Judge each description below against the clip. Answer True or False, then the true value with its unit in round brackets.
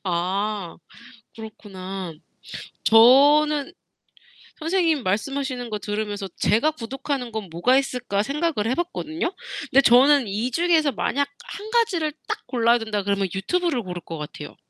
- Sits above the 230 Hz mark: True (245 Hz)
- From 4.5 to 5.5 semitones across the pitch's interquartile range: False (6.5 semitones)